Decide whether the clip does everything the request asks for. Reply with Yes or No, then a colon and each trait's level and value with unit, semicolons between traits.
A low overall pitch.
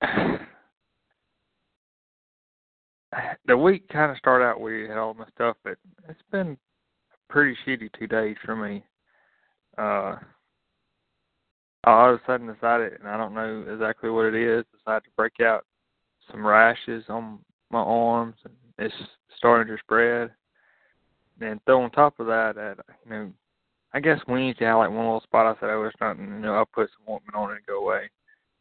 Yes: low, 115 Hz